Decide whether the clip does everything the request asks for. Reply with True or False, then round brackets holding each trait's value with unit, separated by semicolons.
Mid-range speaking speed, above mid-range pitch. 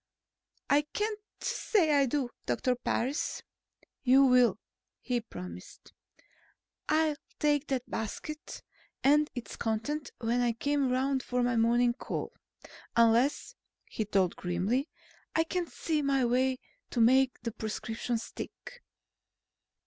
False (125 wpm; 255 Hz)